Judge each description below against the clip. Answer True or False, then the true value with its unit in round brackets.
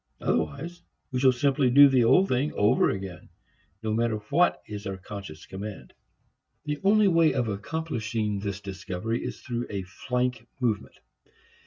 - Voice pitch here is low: True (120 Hz)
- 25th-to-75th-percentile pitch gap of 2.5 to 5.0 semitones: False (5.5 semitones)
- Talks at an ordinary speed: True (150 wpm)